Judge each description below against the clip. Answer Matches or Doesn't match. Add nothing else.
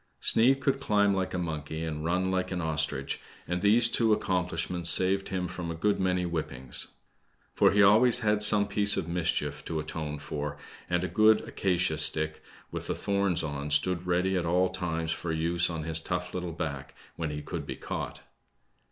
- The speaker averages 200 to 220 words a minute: Doesn't match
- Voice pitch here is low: Matches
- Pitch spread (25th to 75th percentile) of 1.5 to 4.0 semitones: Matches